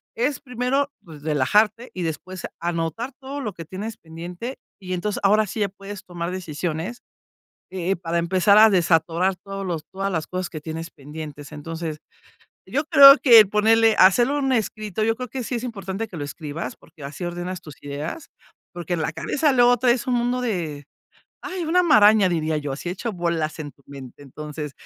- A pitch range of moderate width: No, wide, 5.8 semitones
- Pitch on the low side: No, medium, 185 Hz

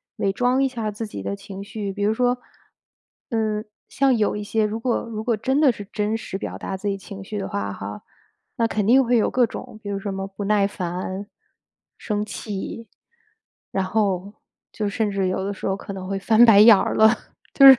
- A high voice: Yes, high, 210 Hz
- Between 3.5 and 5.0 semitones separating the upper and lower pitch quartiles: No, narrow, 2.5 semitones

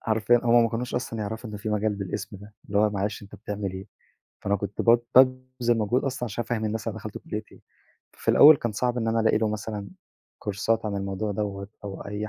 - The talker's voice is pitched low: Yes, low, 110 Hz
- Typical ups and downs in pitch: No, narrow, 2.3 semitones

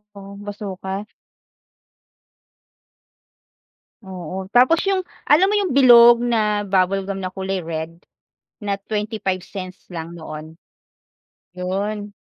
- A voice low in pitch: No, high, 195 Hz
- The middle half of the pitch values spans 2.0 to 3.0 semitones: Yes, narrow, 2.6 semitones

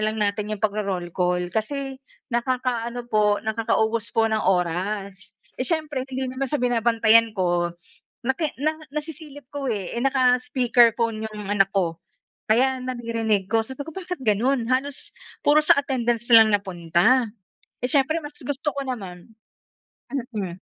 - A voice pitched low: No, high, 230 Hz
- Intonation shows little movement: No, average, 4.2 semitones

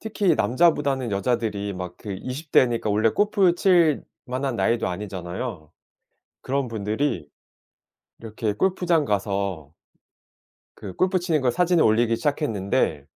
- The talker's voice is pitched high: No, low, 120 Hz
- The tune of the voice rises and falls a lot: Yes, wide, 7.3 semitones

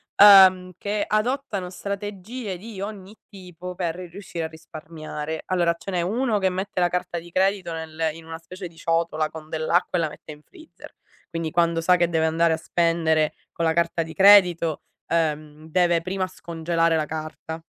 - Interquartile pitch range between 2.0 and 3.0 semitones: Yes, narrow, 2.6 semitones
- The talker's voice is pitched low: No, medium, 170 Hz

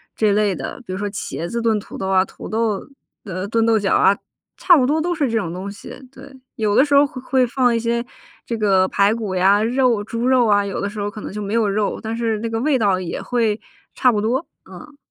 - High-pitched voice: Yes, high, 220 Hz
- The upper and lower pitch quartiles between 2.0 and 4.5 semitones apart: Yes, average, 3.5 semitones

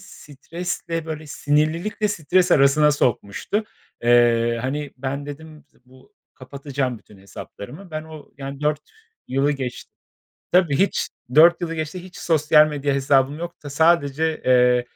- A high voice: No, medium, 150 Hz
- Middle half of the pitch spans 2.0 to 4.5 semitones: Yes, average, 3.2 semitones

